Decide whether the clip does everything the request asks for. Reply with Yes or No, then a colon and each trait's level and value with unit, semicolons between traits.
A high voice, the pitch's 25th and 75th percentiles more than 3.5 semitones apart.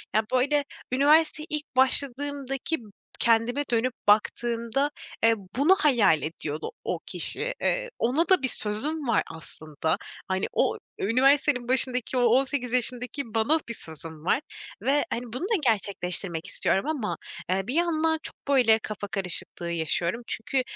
Yes: high, 245 Hz; wide, 5.5 semitones